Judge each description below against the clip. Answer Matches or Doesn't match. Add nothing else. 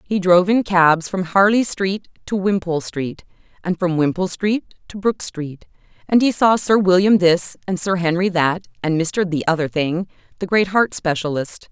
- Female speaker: Matches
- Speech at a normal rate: Matches